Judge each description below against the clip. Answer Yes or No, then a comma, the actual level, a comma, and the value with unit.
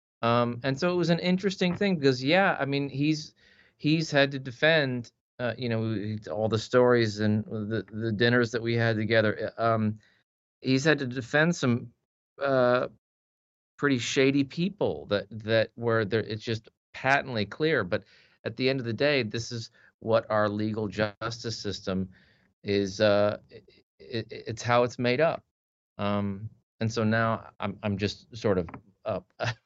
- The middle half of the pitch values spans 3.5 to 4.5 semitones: Yes, average, 3.8 semitones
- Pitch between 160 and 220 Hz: No, low, 115 Hz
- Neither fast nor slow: Yes, average, 165 wpm